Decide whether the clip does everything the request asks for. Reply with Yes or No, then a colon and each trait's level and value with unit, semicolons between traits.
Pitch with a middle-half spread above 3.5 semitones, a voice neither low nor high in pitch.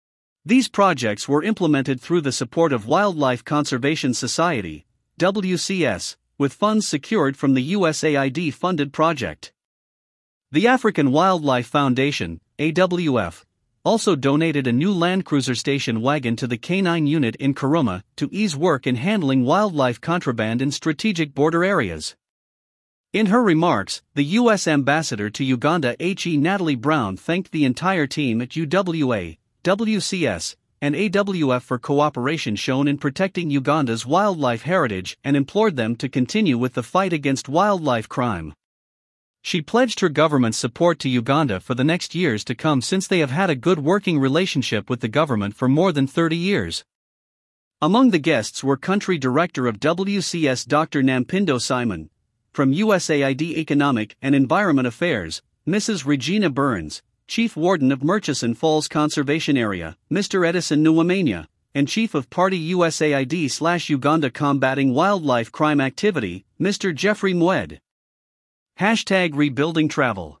Yes: wide, 5.4 semitones; medium, 150 Hz